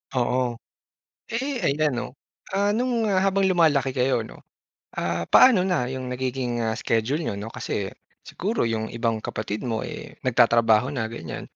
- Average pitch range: No, wide, 7.3 semitones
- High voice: No, low, 125 Hz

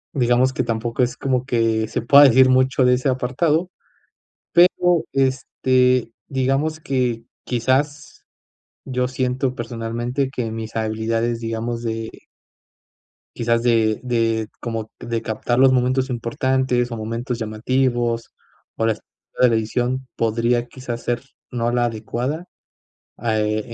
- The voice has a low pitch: Yes, low, 120 Hz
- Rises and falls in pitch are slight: Yes, narrow, 2.2 semitones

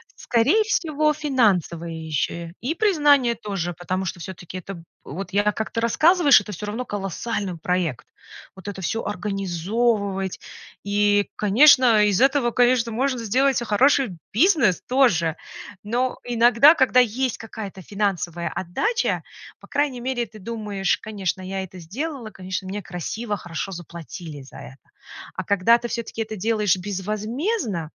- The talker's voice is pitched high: Yes, high, 210 Hz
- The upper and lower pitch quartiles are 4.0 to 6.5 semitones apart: Yes, average, 4.9 semitones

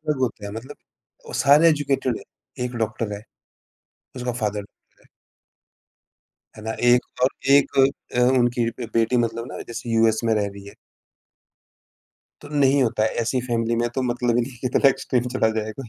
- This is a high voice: No, low, 120 Hz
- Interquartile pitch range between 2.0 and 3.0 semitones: Yes, narrow, 2.4 semitones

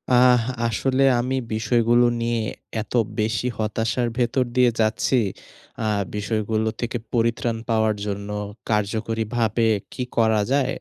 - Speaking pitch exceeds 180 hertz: No, low, 115 Hz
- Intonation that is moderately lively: No, narrow, 2.0 semitones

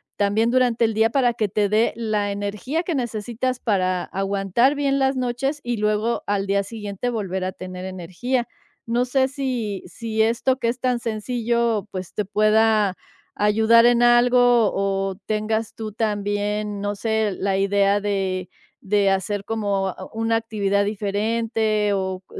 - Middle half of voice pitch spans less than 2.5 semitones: No, average, 2.9 semitones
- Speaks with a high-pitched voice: Yes, high, 215 Hz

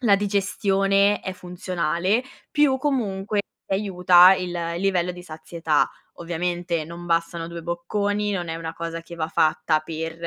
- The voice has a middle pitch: Yes, medium, 180 Hz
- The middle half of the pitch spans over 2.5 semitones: Yes, average, 2.9 semitones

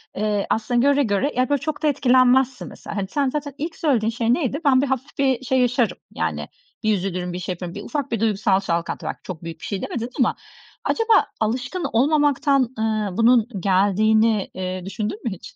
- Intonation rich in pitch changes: No, average, 4.9 semitones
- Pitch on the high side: Yes, high, 235 Hz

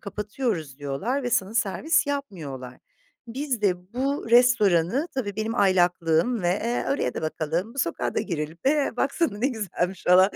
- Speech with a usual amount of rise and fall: No, wide, 6.3 semitones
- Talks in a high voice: Yes, high, 205 Hz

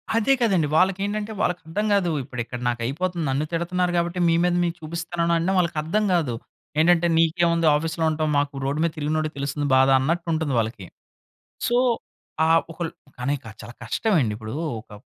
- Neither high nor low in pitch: Yes, medium, 165 Hz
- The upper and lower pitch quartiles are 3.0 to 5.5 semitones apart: Yes, average, 3.7 semitones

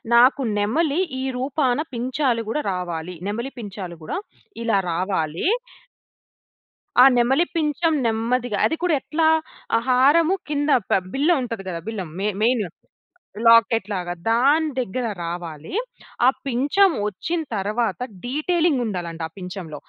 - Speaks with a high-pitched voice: Yes, high, 235 Hz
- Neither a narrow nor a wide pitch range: No, wide, 6.8 semitones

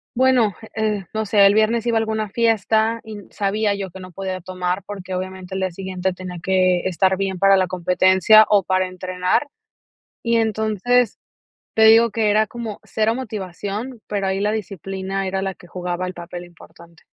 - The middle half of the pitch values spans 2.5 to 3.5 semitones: Yes, average, 2.8 semitones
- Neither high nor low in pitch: No, high, 195 Hz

